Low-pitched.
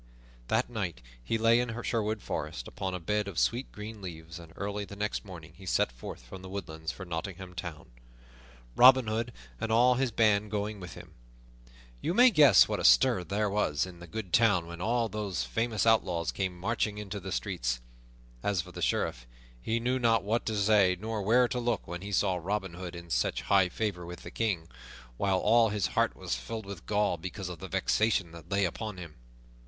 Yes: low, 100 Hz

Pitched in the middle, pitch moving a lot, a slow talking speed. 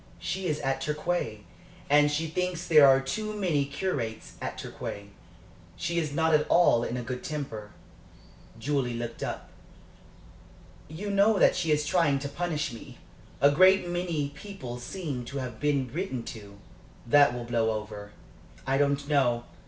No: medium, 145 Hz; wide, 5.7 semitones; average, 160 wpm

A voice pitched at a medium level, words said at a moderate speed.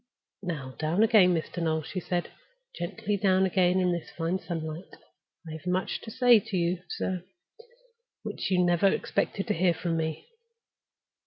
Yes: medium, 180 Hz; average, 160 wpm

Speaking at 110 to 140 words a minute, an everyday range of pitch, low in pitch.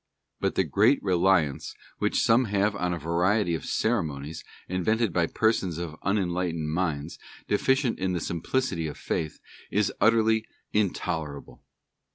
Yes: slow, 135 wpm; average, 4.5 semitones; very low, 90 Hz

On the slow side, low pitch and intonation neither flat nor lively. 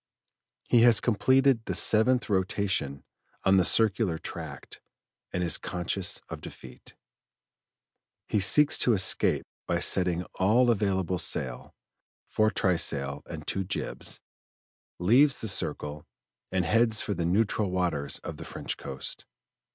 Yes: slow, 125 wpm; very low, 95 Hz; average, 4.2 semitones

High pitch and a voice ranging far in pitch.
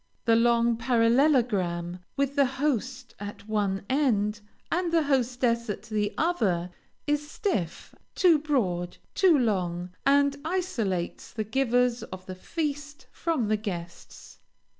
Yes: high, 235 Hz; wide, 5.8 semitones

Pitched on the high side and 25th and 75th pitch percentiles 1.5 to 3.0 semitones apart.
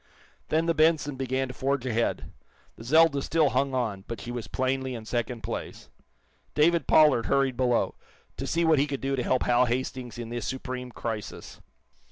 No: low, 130 Hz; average, 2.7 semitones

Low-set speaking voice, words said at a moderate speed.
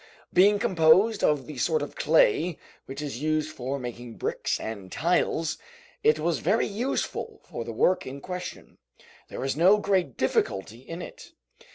No: medium, 170 Hz; average, 160 wpm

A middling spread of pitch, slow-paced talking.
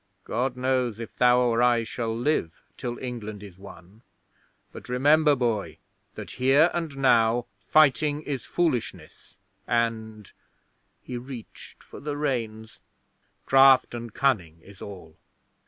Yes: average, 3.5 semitones; slow, 125 wpm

